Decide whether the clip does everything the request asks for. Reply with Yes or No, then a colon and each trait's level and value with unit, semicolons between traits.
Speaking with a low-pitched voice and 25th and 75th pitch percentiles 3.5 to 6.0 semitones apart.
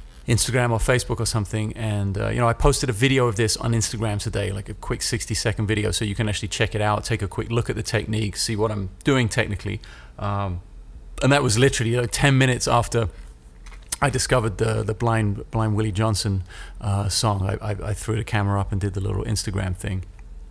No: low, 110 Hz; narrow, 2.5 semitones